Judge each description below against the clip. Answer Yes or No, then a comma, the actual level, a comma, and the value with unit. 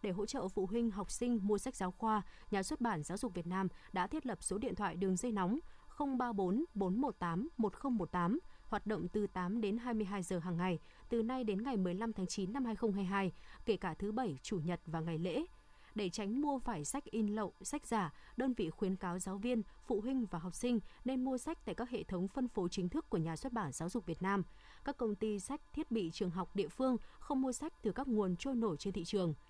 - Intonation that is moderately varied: Yes, average, 4.8 semitones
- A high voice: Yes, high, 210 Hz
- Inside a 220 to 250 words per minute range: Yes, average, 240 wpm